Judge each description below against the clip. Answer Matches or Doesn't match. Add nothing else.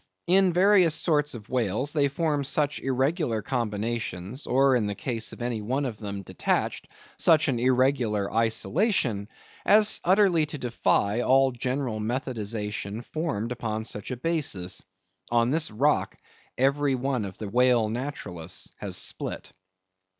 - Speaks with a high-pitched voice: Doesn't match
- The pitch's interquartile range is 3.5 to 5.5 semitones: Matches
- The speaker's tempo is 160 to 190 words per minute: Doesn't match